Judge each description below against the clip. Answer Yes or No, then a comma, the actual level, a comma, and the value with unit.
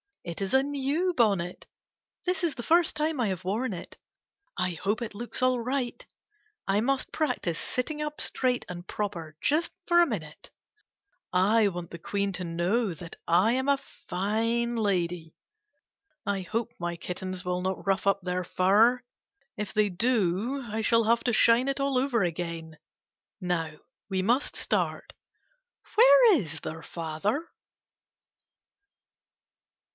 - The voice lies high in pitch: Yes, high, 210 Hz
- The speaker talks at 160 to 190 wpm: No, average, 150 wpm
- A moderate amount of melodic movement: No, wide, 6.0 semitones